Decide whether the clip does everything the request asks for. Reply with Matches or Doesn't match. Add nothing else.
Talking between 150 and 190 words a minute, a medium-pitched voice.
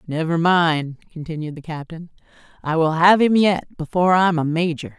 Matches